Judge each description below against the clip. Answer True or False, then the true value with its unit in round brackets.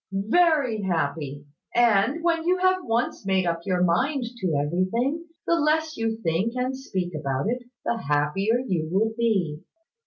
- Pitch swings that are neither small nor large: False (7.3 semitones)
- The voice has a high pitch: True (220 Hz)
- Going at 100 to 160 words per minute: True (155 wpm)